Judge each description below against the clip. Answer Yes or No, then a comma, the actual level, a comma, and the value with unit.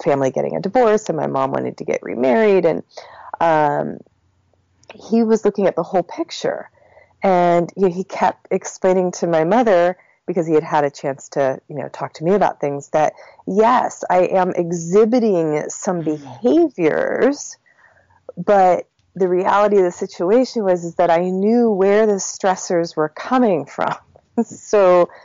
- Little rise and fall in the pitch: No, average, 4.4 semitones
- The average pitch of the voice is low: No, medium, 180 Hz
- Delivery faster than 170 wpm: No, average, 160 wpm